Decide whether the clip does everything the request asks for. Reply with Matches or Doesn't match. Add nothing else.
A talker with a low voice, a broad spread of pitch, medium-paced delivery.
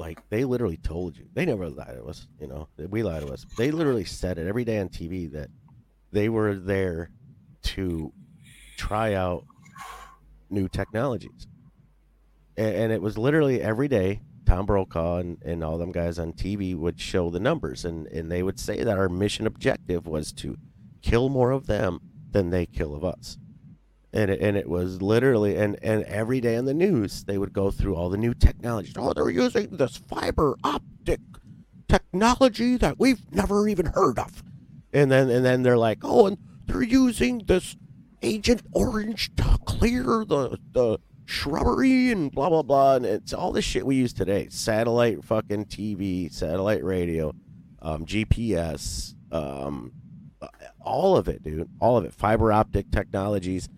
Matches